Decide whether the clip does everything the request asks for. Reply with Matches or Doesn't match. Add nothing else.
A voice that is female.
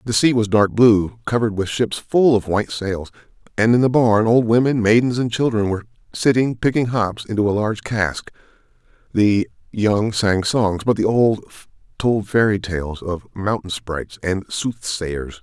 Doesn't match